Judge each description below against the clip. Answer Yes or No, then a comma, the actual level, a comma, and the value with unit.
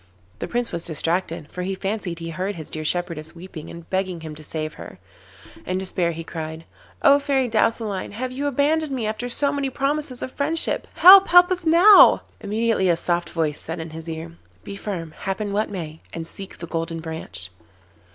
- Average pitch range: No, wide, 7.2 semitones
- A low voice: No, medium, 185 Hz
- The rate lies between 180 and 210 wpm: Yes, average, 190 wpm